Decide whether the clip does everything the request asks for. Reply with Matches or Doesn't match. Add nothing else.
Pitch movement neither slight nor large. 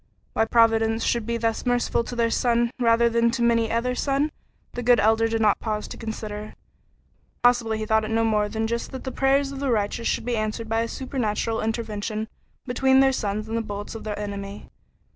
Doesn't match